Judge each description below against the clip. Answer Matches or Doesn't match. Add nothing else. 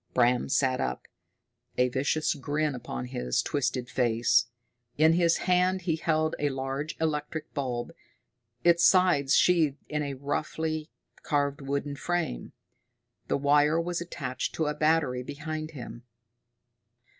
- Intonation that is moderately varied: Matches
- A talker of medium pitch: Matches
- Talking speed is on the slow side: Matches